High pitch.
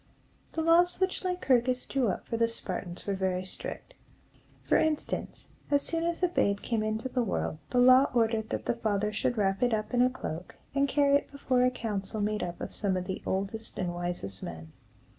Yes: high, 225 Hz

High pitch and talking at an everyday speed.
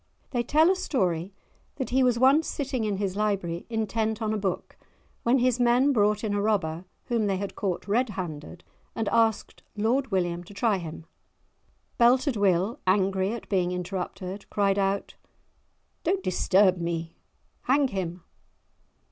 Yes: high, 205 Hz; average, 150 wpm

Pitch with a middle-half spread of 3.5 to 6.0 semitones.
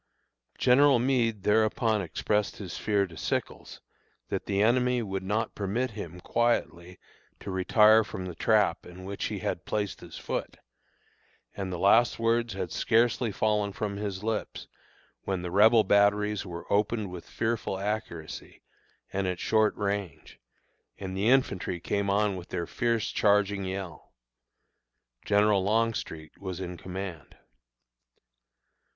No: average, 2.9 semitones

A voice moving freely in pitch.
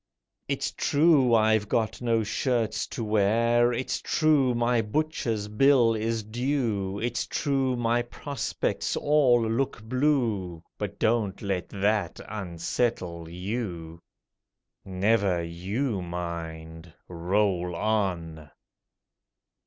No: average, 4.8 semitones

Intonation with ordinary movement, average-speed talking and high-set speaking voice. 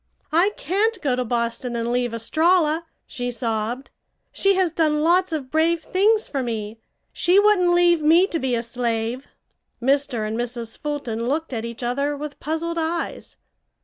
No: wide, 5.9 semitones; average, 165 wpm; very high, 285 Hz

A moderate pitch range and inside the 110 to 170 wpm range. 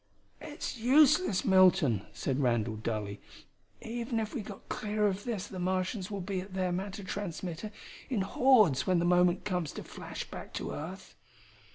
Yes: average, 3.4 semitones; average, 165 wpm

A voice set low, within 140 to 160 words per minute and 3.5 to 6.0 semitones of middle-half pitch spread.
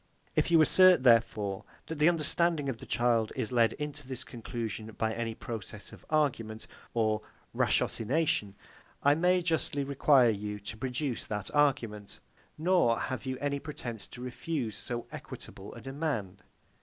Yes: low, 125 Hz; average, 150 wpm; average, 5.0 semitones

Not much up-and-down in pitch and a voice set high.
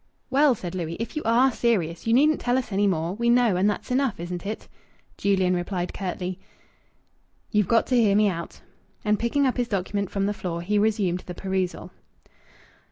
No: average, 4.6 semitones; high, 205 Hz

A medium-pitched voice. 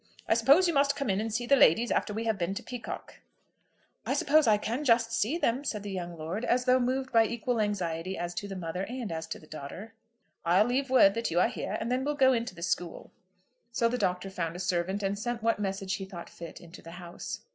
No: high, 210 Hz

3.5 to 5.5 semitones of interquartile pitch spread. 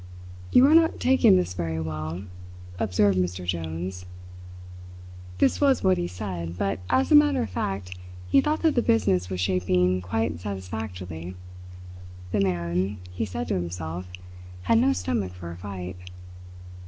No: narrow, 2.4 semitones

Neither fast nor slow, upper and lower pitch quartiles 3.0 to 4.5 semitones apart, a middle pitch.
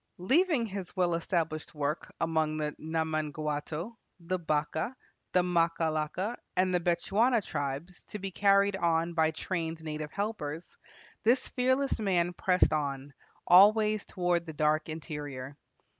No: slow, 130 wpm; average, 4.0 semitones; medium, 170 Hz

